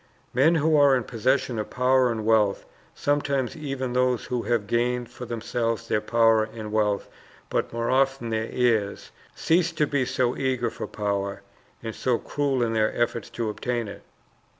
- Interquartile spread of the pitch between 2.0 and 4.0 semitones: Yes, average, 2.9 semitones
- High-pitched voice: No, low, 120 Hz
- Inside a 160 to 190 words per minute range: Yes, average, 175 wpm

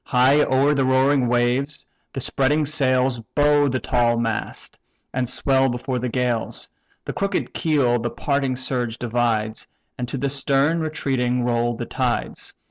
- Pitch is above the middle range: No, low, 130 Hz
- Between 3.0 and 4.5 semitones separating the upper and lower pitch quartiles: No, narrow, 2.4 semitones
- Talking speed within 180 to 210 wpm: No, average, 150 wpm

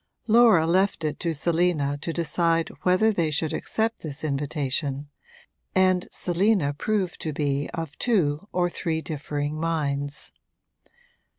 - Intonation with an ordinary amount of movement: Yes, average, 3.8 semitones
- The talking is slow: Yes, slow, 125 wpm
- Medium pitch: Yes, medium, 160 Hz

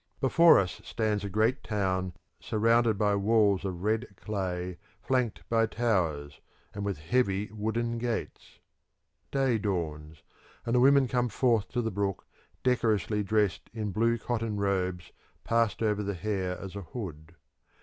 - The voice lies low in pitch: Yes, low, 105 Hz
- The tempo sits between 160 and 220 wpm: No, average, 145 wpm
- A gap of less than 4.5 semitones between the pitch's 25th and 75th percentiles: Yes, average, 3.5 semitones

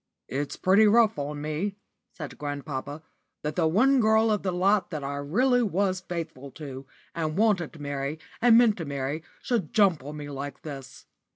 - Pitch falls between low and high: Yes, medium, 160 Hz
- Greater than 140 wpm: Yes, average, 180 wpm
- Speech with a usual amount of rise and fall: No, wide, 6.2 semitones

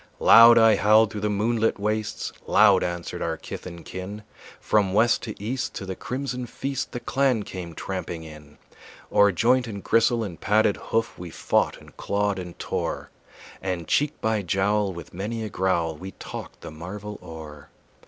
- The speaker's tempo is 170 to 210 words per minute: Yes, average, 175 wpm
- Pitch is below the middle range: Yes, low, 105 Hz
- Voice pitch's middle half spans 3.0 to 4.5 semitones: Yes, average, 3.6 semitones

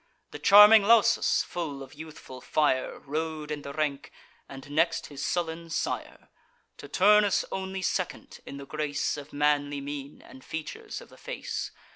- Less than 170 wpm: Yes, average, 155 wpm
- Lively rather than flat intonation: No, average, 3.5 semitones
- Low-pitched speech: No, medium, 155 Hz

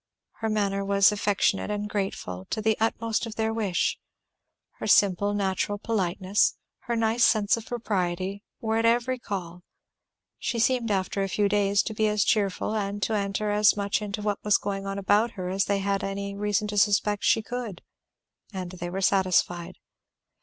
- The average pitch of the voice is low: No, high, 205 Hz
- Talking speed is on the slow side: No, average, 175 wpm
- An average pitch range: No, narrow, 1.8 semitones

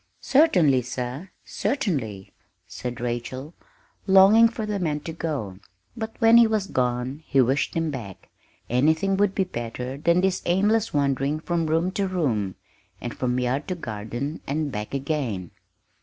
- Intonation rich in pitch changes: Yes, wide, 7.2 semitones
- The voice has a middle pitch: Yes, medium, 150 Hz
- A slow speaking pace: No, average, 150 wpm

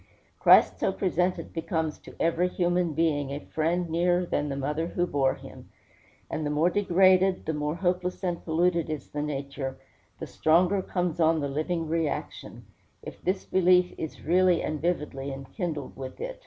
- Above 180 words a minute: No, average, 170 wpm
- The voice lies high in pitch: No, medium, 165 Hz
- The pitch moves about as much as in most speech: Yes, average, 3.2 semitones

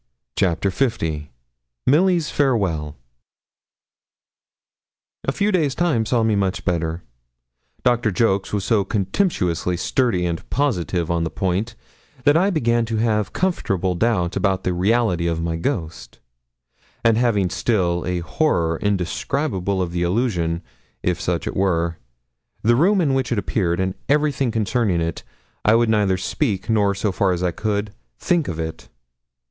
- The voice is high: No, low, 100 Hz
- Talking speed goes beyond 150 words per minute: No, average, 145 wpm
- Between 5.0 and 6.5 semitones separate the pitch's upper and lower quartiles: Yes, wide, 5.4 semitones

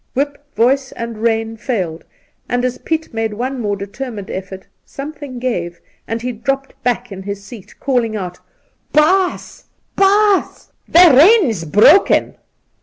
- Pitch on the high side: Yes, high, 245 Hz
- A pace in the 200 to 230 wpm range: No, average, 140 wpm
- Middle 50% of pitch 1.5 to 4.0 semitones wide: No, average, 5.1 semitones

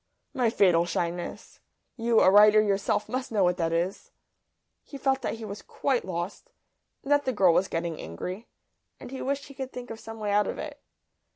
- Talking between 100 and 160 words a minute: No, average, 200 wpm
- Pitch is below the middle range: No, high, 210 Hz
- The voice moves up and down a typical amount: No, wide, 6.1 semitones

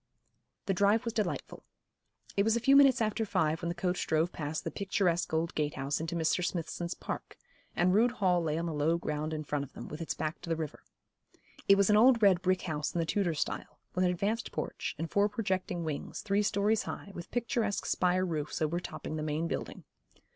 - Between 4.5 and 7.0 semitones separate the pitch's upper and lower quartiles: No, average, 4.1 semitones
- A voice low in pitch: No, medium, 175 Hz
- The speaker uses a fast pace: Yes, fast, 215 wpm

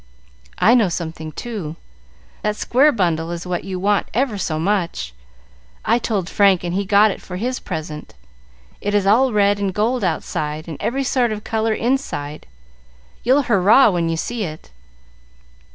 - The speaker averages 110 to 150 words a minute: No, average, 165 wpm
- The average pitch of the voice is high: Yes, high, 200 Hz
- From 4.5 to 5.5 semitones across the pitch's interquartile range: Yes, average, 5.1 semitones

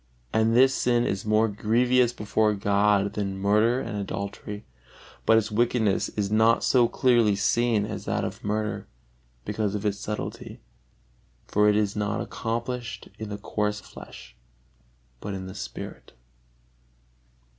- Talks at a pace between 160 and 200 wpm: No, average, 140 wpm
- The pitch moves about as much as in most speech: No, narrow, 2.1 semitones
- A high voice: No, low, 105 Hz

